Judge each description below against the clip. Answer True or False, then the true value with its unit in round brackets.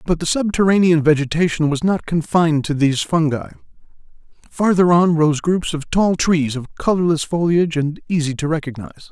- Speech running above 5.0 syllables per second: True (5.5 syllables/s)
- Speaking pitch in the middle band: True (160 Hz)